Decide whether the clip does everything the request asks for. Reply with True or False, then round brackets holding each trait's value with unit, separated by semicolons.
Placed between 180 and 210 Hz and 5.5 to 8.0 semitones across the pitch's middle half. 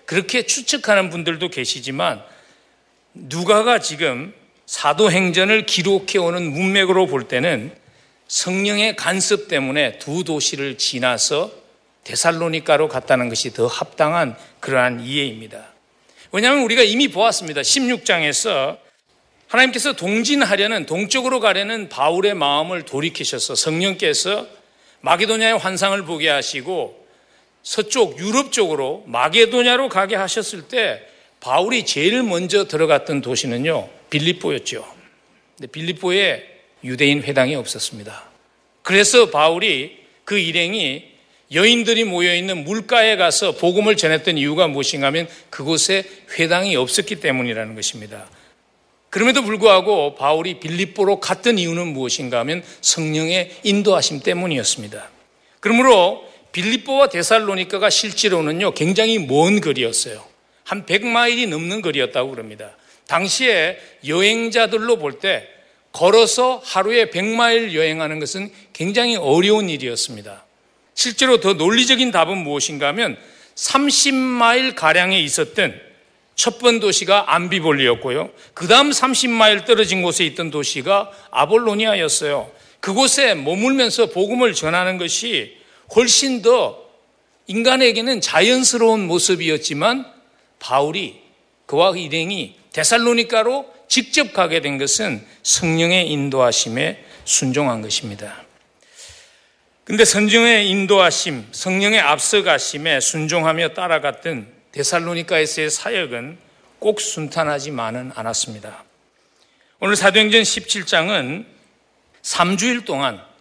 True (190 Hz; 6.5 semitones)